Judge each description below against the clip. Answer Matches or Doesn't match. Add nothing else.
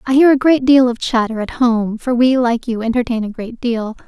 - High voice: Matches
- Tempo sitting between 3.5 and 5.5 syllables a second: Matches